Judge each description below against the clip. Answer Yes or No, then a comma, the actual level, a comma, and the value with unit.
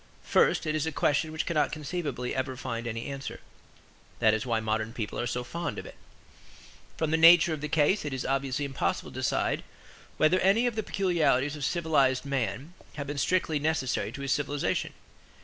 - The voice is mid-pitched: Yes, medium, 145 Hz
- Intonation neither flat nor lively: Yes, average, 3.8 semitones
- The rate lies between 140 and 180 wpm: No, average, 190 wpm